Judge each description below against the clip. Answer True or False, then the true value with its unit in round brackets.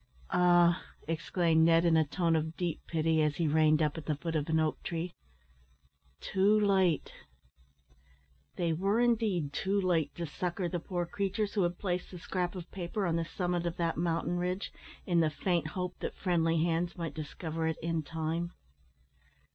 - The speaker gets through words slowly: False (180 wpm)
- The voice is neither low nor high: True (170 Hz)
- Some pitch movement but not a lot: False (2.0 semitones)